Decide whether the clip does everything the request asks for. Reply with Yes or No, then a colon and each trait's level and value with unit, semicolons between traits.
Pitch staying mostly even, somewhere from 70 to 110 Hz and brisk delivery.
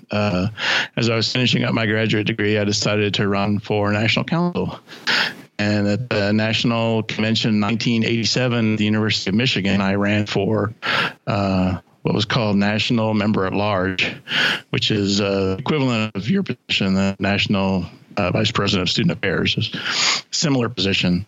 No: narrow, 2.2 semitones; low, 105 Hz; average, 160 wpm